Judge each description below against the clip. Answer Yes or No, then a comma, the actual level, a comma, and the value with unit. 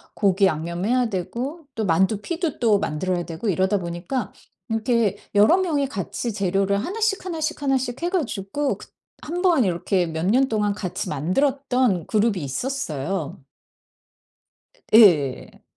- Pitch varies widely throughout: Yes, wide, 6.9 semitones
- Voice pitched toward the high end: Yes, high, 210 Hz